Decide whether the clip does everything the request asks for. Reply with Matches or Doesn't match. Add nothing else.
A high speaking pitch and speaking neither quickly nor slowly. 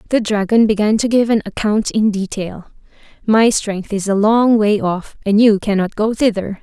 Matches